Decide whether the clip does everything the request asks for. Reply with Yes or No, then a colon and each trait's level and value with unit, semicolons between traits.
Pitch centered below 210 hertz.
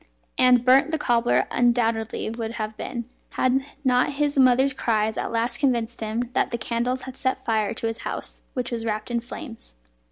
No: high, 240 Hz